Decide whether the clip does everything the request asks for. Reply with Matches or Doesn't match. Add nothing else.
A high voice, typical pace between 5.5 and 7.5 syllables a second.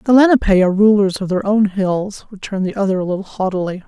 Matches